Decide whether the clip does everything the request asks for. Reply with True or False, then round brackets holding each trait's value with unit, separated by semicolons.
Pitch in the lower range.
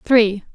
False (220 Hz)